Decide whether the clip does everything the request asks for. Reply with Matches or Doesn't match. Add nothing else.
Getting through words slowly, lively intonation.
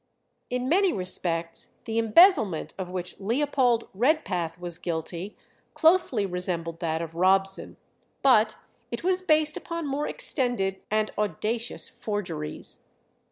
Matches